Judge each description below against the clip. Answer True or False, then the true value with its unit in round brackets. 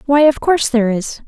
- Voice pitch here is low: False (260 Hz)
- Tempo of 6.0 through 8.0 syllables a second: True (6.3 syllables/s)